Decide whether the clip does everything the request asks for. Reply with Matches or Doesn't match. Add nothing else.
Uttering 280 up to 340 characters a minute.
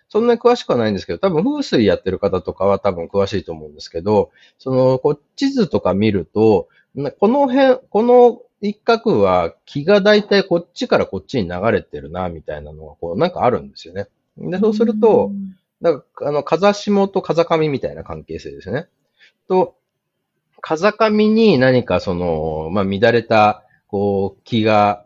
Matches